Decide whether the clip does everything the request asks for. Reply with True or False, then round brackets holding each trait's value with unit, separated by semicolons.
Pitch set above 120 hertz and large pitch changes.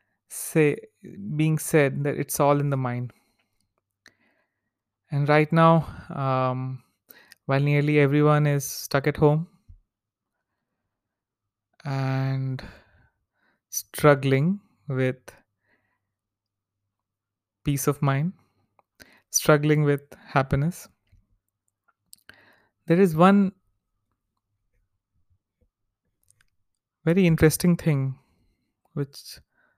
True (135 Hz; 6.9 semitones)